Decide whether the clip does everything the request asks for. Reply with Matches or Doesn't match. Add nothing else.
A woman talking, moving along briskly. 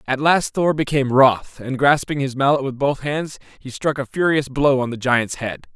Doesn't match